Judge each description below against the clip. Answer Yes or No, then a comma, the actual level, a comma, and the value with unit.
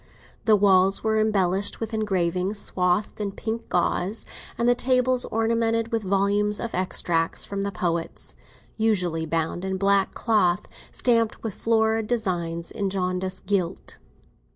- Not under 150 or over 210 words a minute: No, slow, 135 wpm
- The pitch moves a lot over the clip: No, average, 3.5 semitones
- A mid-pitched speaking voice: No, high, 200 Hz